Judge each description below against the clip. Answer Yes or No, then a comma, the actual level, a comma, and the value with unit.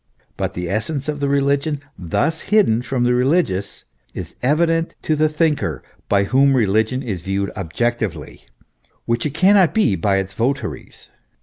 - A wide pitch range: Yes, wide, 7.2 semitones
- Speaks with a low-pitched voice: Yes, low, 130 Hz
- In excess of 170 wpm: No, average, 150 wpm